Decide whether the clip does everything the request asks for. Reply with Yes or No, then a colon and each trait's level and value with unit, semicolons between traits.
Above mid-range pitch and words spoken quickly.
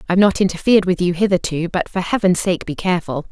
No: medium, 180 Hz; fast, 215 wpm